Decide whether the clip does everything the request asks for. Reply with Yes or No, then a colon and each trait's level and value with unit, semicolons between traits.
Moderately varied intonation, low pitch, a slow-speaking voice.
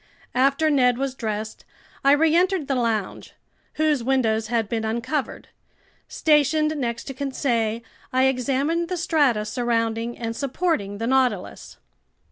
No: average, 4.2 semitones; very high, 260 Hz; slow, 125 wpm